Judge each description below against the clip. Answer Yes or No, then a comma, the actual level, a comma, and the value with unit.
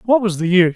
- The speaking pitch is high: Yes, high, 195 Hz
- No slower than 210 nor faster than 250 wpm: No, fast, 315 wpm